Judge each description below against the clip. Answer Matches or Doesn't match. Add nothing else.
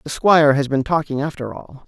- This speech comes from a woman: Doesn't match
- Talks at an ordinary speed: Doesn't match